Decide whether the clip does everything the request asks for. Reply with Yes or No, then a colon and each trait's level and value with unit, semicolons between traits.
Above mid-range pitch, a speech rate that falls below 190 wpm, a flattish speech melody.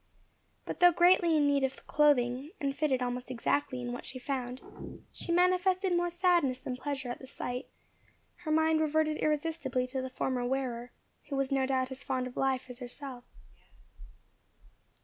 No: very high, 270 Hz; average, 170 wpm; average, 3.6 semitones